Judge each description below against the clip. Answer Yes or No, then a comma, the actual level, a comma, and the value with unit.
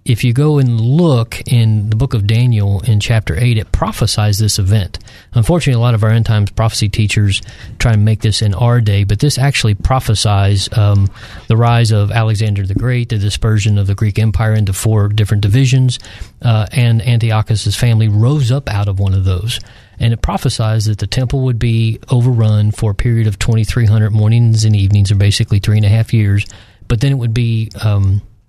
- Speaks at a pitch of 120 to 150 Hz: No, low, 110 Hz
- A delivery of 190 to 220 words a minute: Yes, average, 200 wpm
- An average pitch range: No, narrow, 2.3 semitones